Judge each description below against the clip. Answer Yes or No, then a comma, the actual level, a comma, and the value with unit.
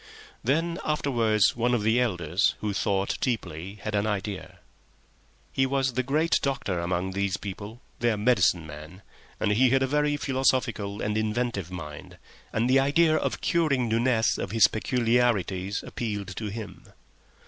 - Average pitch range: Yes, average, 4.6 semitones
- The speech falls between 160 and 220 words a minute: No, average, 150 wpm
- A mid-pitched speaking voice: No, low, 110 Hz